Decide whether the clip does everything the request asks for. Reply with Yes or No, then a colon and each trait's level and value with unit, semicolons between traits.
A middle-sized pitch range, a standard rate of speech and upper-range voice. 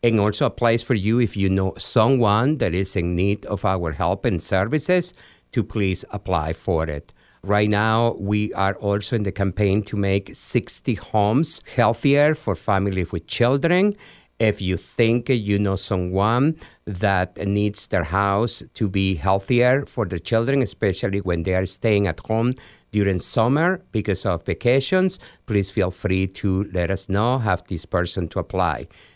No: average, 3.6 semitones; average, 165 wpm; low, 100 Hz